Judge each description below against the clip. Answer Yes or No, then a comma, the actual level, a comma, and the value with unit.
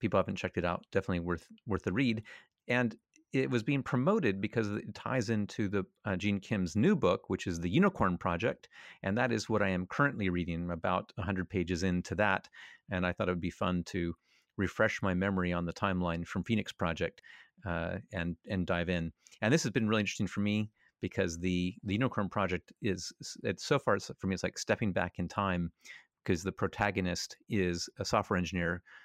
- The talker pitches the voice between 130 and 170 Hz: No, very low, 95 Hz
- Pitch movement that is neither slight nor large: Yes, average, 3.1 semitones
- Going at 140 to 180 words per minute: No, average, 200 wpm